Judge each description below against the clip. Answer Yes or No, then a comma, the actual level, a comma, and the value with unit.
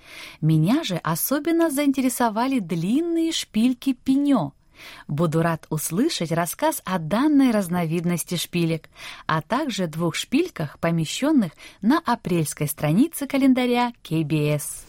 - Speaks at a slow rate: Yes, slow, 100 wpm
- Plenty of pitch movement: Yes, wide, 8.7 semitones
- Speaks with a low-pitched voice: No, high, 205 Hz